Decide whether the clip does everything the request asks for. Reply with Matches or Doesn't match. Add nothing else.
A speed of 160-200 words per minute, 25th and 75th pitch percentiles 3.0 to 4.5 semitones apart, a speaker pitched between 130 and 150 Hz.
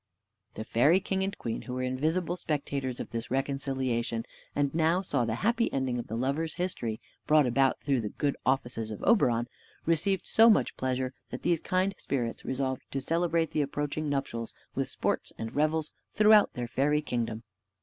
Doesn't match